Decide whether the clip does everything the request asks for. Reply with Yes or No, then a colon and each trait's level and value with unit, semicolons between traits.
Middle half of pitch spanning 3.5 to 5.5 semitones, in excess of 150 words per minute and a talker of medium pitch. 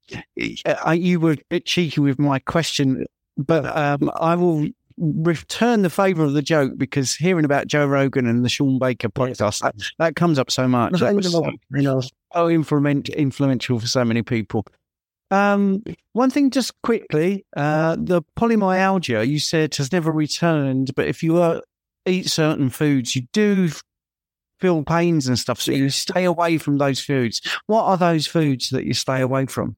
Yes: average, 4.5 semitones; average, 165 wpm; medium, 150 Hz